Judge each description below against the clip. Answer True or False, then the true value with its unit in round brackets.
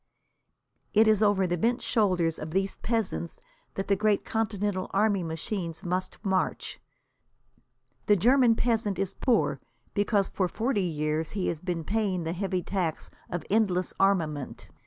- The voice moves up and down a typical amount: True (3.4 semitones)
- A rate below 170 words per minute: True (145 wpm)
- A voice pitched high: True (195 Hz)